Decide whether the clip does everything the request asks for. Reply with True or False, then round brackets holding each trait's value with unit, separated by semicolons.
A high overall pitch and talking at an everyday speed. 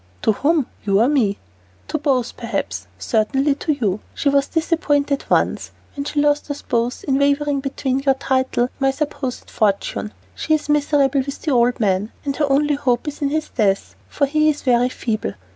True (275 Hz; 190 wpm)